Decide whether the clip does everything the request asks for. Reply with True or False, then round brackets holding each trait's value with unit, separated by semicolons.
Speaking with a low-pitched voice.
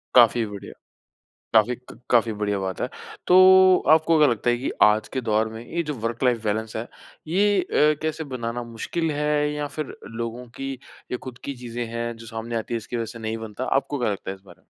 True (120 Hz)